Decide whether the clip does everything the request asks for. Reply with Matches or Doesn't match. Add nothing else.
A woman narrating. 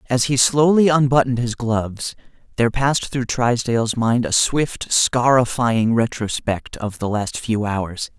Doesn't match